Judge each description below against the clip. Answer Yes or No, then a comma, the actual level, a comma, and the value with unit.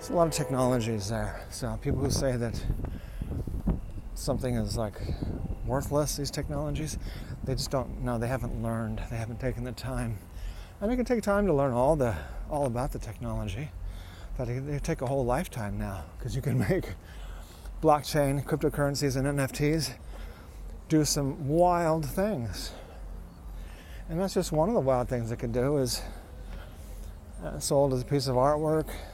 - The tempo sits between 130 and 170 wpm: Yes, average, 165 wpm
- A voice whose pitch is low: Yes, low, 125 Hz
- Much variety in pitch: Yes, wide, 7.6 semitones